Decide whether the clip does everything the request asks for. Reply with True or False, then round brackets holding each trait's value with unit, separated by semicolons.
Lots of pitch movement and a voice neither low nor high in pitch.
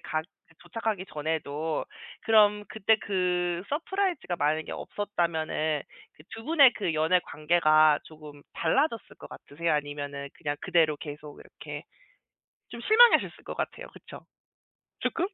True (5.7 semitones; 170 Hz)